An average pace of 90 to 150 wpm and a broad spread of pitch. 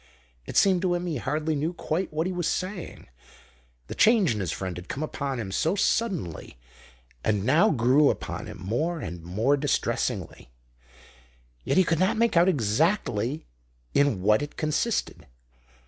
No: average, 165 wpm; wide, 8.3 semitones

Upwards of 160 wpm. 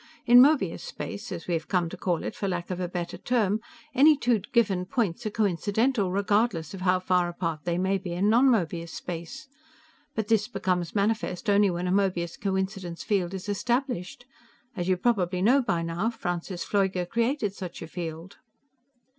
Yes: average, 180 wpm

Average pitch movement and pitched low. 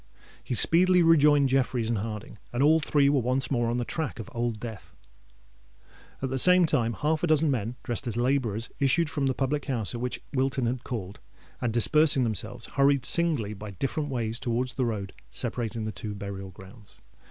Yes: average, 3.9 semitones; low, 125 Hz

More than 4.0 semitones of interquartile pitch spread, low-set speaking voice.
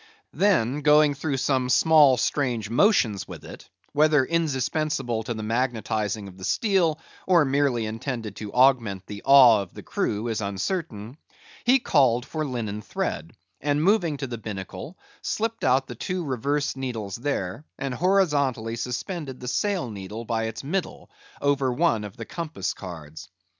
Yes: average, 5.2 semitones; low, 130 Hz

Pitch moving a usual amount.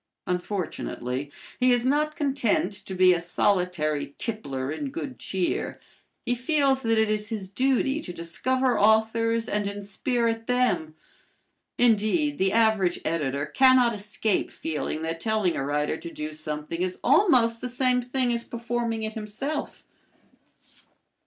No: wide, 6.0 semitones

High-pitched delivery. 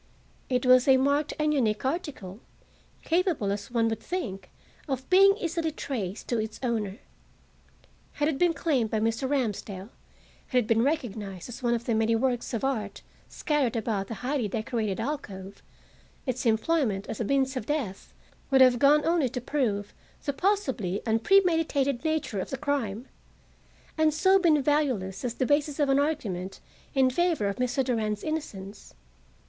Yes: very high, 255 Hz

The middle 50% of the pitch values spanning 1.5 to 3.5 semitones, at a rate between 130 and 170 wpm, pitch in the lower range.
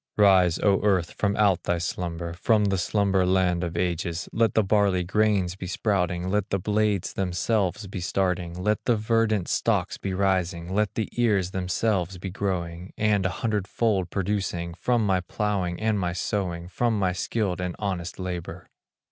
Yes: average, 2.9 semitones; average, 165 wpm; very low, 95 Hz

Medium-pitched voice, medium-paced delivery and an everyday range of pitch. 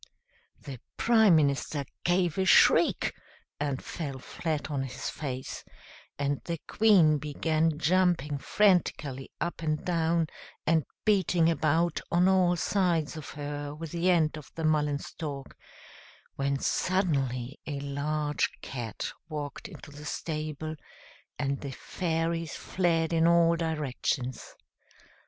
No: medium, 155 Hz; slow, 125 wpm; average, 3.0 semitones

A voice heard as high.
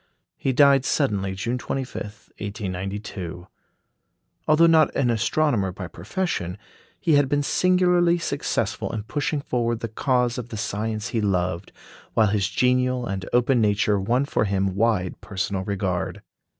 No: low, 110 Hz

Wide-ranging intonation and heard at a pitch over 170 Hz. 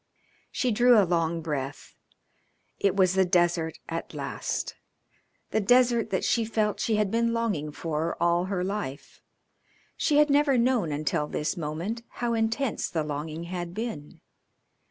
Yes: wide, 6.1 semitones; high, 190 Hz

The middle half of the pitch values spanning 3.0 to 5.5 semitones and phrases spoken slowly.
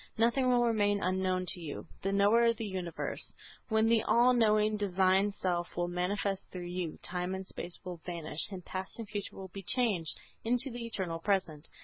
No: average, 3.6 semitones; average, 190 wpm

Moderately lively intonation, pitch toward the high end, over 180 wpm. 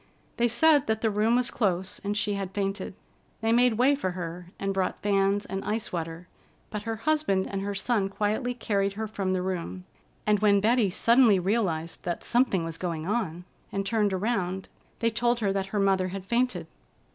Yes: average, 3.3 semitones; high, 200 Hz; average, 190 wpm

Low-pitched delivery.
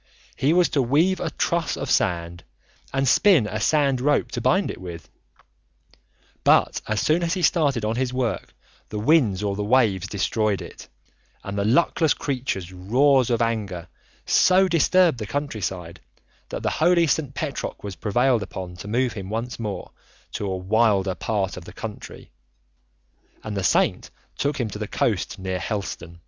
Yes: low, 115 Hz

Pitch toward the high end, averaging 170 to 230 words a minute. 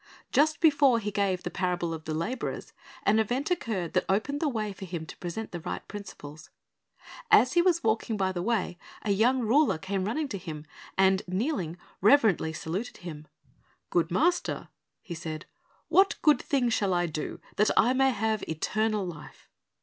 Yes: high, 205 Hz; average, 175 wpm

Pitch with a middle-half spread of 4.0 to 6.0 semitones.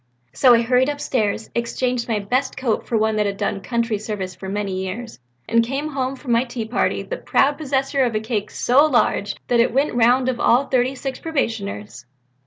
No: average, 3.5 semitones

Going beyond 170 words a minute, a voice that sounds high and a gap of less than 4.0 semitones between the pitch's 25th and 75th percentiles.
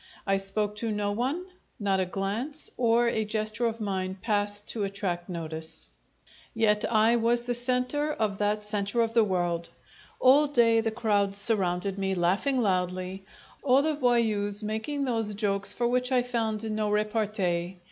No: average, 160 wpm; high, 215 Hz; average, 3.3 semitones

